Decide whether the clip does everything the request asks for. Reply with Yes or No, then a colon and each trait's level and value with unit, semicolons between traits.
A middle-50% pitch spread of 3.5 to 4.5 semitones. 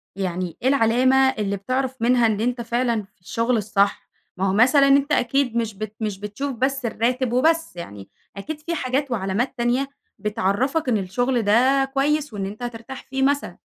Yes: average, 4.2 semitones